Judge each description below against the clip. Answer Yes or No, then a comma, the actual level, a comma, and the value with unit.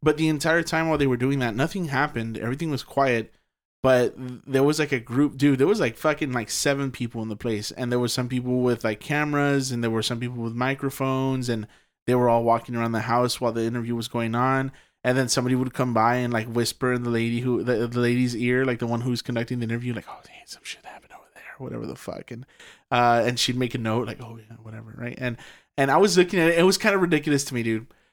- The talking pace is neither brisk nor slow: No, fast, 260 wpm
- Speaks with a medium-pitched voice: No, low, 125 Hz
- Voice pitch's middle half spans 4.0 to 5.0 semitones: No, average, 2.7 semitones